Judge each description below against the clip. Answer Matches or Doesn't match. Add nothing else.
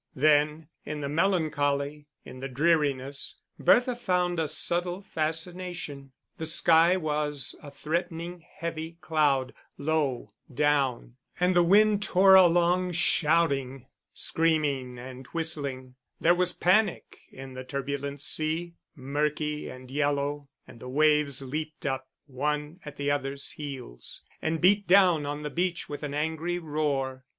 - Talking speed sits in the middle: Doesn't match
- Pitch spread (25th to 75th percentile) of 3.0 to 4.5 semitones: Matches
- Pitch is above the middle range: Doesn't match